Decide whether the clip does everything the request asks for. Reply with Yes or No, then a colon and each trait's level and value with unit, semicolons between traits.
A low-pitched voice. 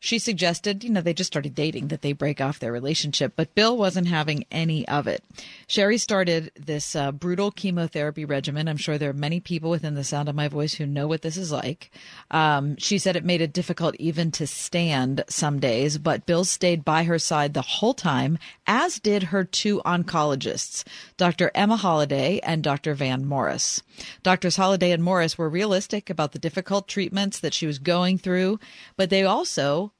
No: medium, 165 Hz